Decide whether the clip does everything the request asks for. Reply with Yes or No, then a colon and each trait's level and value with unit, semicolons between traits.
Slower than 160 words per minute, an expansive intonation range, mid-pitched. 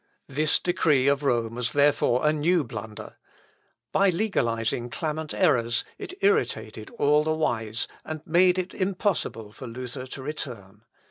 Yes: average, 140 wpm; wide, 5.8 semitones; medium, 145 Hz